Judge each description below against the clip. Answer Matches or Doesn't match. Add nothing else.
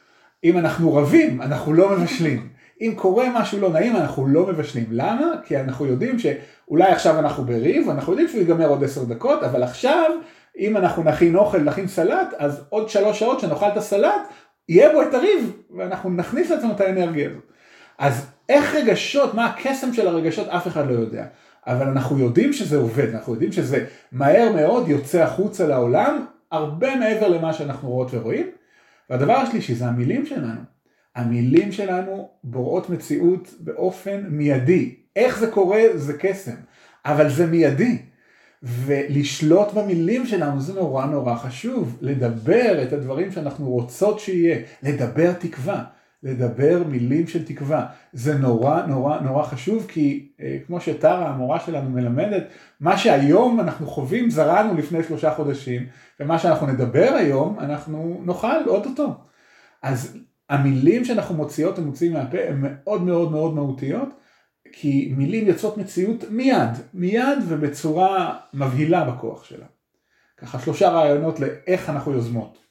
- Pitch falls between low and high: Matches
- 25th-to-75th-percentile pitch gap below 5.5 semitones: Doesn't match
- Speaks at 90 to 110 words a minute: Doesn't match